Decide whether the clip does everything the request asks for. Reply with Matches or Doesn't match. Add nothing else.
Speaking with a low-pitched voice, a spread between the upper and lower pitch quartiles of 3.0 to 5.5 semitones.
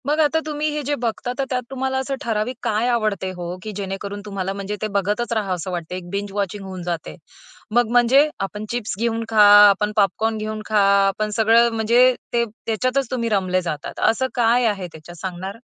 Doesn't match